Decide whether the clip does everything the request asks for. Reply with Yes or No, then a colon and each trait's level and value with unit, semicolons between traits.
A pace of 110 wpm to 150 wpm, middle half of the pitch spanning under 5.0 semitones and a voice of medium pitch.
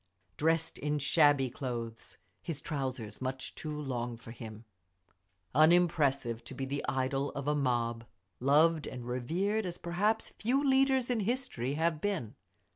No: average, 140 wpm; average, 5.3 semitones; medium, 145 Hz